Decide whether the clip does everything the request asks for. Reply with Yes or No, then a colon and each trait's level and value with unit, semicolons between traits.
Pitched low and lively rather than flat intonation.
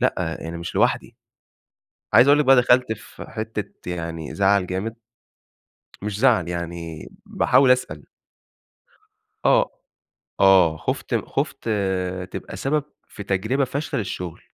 Yes: low, 100 Hz; wide, 6.6 semitones